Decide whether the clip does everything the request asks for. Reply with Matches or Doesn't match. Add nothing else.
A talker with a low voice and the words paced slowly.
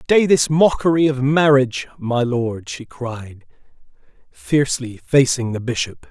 Matches